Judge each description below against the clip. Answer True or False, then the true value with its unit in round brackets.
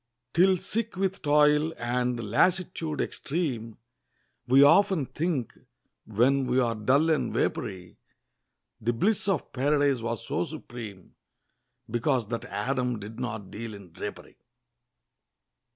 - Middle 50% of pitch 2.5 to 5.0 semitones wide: False (5.4 semitones)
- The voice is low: True (130 Hz)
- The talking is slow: True (120 wpm)